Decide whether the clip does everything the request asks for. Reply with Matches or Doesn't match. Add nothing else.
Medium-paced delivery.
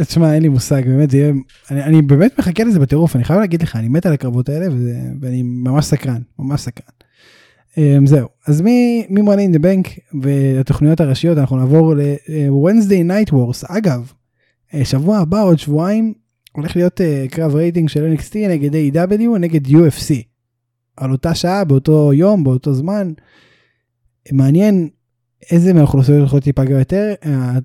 Doesn't match